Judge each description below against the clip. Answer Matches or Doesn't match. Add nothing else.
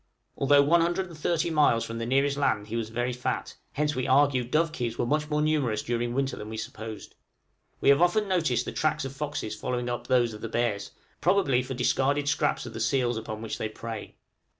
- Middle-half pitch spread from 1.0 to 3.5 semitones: Doesn't match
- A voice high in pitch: Doesn't match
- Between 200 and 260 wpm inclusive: Matches